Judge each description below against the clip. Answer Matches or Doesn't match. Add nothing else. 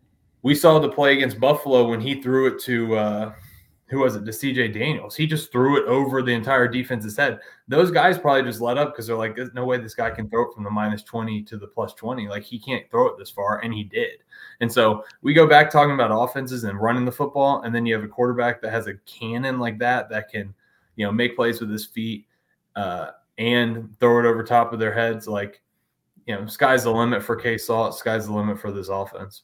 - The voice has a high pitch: Doesn't match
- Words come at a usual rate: Doesn't match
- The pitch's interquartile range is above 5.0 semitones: Doesn't match